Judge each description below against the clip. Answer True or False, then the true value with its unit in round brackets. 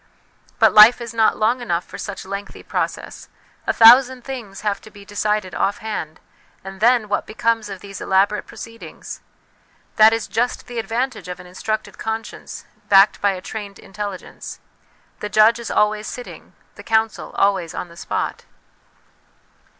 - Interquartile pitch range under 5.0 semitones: True (2.5 semitones)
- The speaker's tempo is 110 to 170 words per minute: True (160 wpm)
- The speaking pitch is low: False (215 Hz)